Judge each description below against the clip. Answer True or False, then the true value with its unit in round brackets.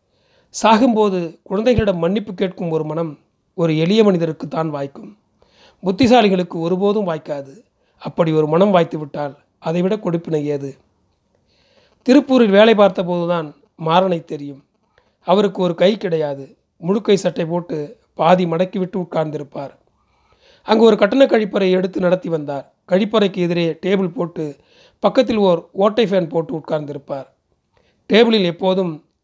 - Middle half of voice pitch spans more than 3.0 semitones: True (4.3 semitones)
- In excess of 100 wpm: True (115 wpm)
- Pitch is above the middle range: False (180 Hz)